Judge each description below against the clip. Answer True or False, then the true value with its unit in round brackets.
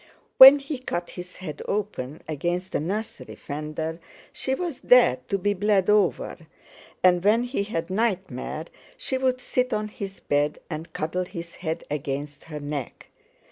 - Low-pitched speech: False (185 Hz)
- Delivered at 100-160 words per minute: True (155 wpm)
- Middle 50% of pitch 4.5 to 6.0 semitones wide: True (5.6 semitones)